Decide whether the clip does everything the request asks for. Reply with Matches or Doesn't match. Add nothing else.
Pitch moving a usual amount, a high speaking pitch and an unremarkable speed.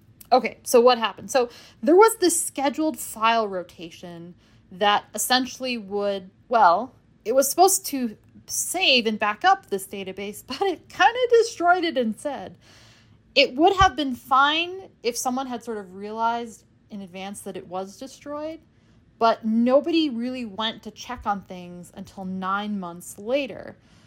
Doesn't match